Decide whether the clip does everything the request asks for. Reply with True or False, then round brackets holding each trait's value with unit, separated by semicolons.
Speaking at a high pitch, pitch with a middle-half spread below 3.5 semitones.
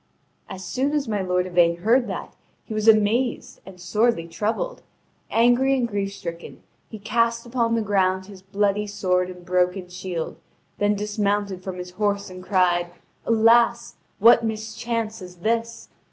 False (205 Hz; 4.0 semitones)